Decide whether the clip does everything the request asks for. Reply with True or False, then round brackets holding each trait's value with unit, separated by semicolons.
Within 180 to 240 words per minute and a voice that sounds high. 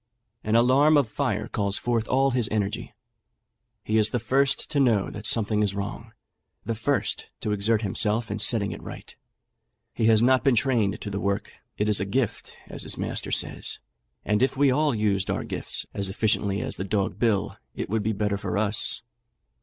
False (195 wpm; 110 Hz)